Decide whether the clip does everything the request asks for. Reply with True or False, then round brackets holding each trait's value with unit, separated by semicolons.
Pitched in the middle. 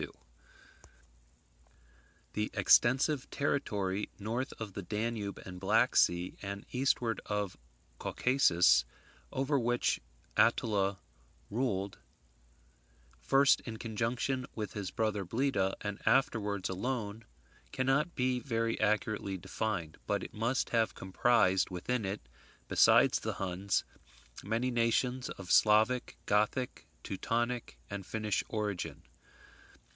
False (110 Hz)